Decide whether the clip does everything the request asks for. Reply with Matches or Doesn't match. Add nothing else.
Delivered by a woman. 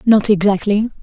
Matches